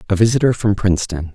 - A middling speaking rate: Yes, average, 180 wpm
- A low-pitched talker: Yes, low, 100 Hz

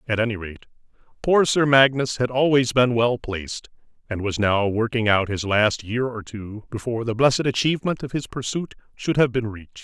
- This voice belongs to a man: Yes, male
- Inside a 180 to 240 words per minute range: Yes, average, 195 wpm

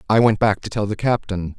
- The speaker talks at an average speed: No, fast, 265 wpm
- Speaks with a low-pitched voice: Yes, low, 105 Hz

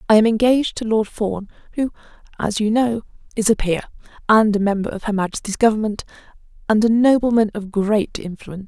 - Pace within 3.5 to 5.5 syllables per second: No, 5.9 syllables/s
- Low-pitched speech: No, high, 215 Hz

